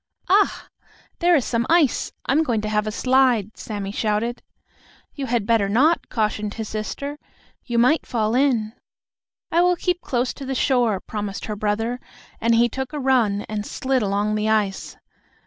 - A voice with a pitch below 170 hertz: No, high, 230 Hz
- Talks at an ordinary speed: Yes, average, 175 wpm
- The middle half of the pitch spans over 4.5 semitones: No, average, 3.9 semitones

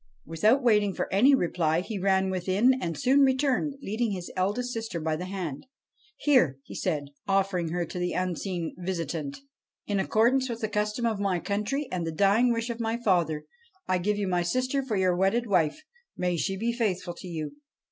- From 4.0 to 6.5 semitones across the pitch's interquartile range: Yes, average, 4.9 semitones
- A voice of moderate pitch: No, high, 195 Hz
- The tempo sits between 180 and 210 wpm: Yes, fast, 205 wpm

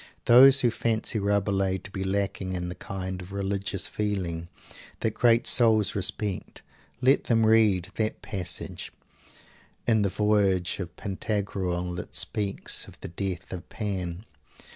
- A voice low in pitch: Yes, low, 100 Hz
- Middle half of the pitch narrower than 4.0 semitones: Yes, narrow, 2.6 semitones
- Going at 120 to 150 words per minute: Yes, average, 140 wpm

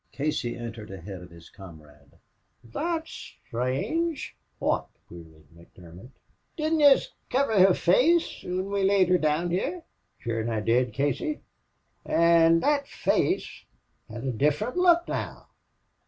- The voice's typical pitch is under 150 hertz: No, medium, 155 Hz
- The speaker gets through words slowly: Yes, slow, 130 wpm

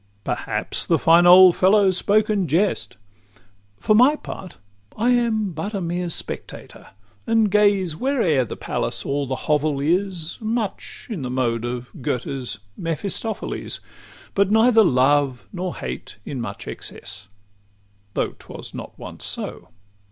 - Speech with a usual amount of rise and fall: No, wide, 7.3 semitones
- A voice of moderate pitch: Yes, medium, 175 Hz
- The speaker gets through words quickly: No, average, 145 wpm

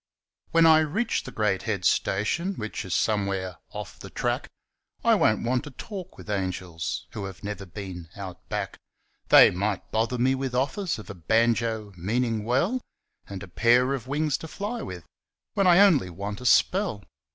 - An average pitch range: No, wide, 6.7 semitones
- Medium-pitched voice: No, low, 110 Hz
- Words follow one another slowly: No, average, 175 wpm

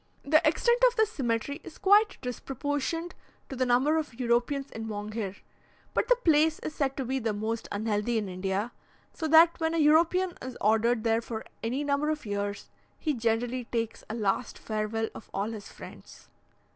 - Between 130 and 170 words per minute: No, average, 180 wpm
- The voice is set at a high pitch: Yes, high, 245 Hz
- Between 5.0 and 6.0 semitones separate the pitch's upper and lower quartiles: Yes, wide, 5.6 semitones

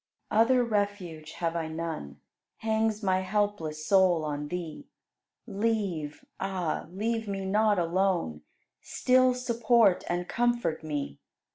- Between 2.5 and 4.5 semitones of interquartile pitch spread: No, average, 5.1 semitones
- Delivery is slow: Yes, slow, 120 wpm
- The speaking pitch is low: No, high, 190 Hz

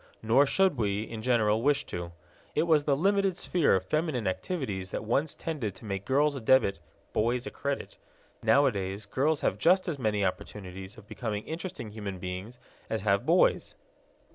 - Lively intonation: Yes, wide, 6.5 semitones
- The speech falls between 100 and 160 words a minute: No, average, 170 wpm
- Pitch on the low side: Yes, low, 115 Hz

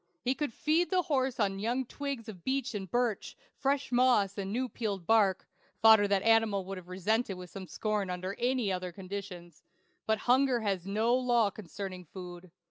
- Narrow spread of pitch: No, average, 4.5 semitones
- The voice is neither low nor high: No, high, 215 Hz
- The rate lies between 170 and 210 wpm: Yes, average, 175 wpm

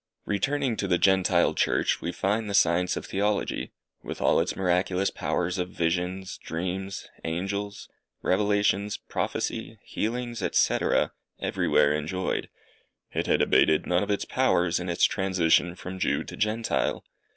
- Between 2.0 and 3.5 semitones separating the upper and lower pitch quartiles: Yes, narrow, 2.5 semitones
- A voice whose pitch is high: No, very low, 95 Hz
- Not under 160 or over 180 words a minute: No, average, 140 wpm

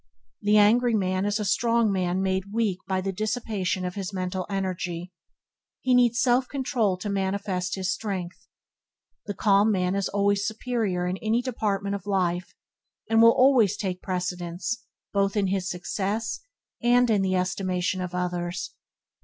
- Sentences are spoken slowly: No, average, 165 wpm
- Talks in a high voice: Yes, high, 195 Hz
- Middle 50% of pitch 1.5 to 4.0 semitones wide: Yes, average, 3.0 semitones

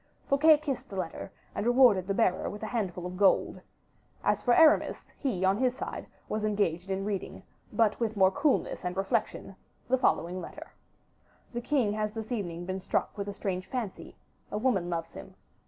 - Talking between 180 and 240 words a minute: Yes, average, 185 wpm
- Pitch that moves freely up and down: No, average, 4.5 semitones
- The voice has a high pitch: Yes, high, 205 Hz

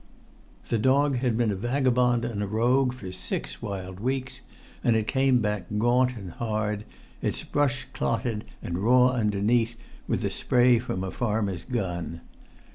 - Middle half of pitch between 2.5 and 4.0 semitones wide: Yes, average, 3.5 semitones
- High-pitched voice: No, low, 115 Hz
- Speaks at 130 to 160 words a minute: Yes, average, 155 wpm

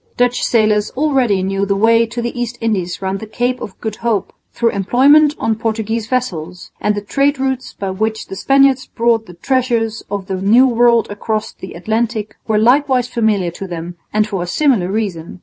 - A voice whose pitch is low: No, high, 220 Hz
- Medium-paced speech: Yes, average, 190 wpm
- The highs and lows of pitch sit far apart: No, average, 3.7 semitones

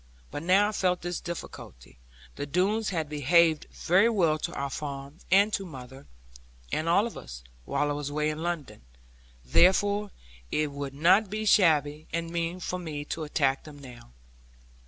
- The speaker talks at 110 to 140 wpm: No, average, 170 wpm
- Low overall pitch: No, medium, 160 Hz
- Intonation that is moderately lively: Yes, average, 4.1 semitones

